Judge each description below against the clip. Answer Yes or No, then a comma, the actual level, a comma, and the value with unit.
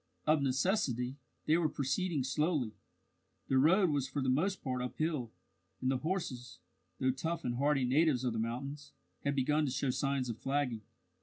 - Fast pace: No, average, 170 wpm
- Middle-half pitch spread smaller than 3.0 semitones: No, average, 3.3 semitones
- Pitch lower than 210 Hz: Yes, low, 135 Hz